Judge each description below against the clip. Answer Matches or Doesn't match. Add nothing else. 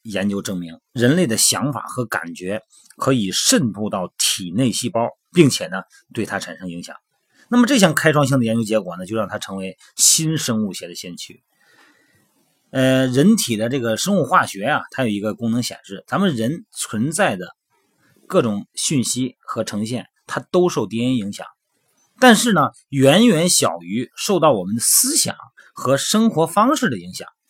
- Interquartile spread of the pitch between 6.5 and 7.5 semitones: Matches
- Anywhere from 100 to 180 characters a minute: Doesn't match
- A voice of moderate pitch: Doesn't match